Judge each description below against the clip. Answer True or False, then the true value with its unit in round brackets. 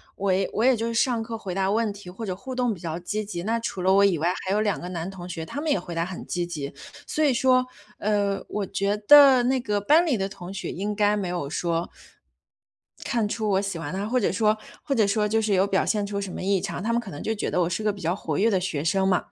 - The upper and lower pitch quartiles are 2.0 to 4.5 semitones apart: True (3.5 semitones)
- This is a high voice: True (200 Hz)